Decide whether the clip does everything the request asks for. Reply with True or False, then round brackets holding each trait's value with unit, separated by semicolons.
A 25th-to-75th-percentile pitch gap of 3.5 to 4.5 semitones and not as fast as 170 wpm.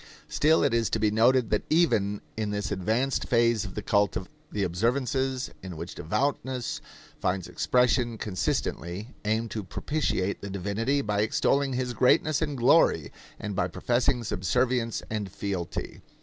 True (4.2 semitones; 150 wpm)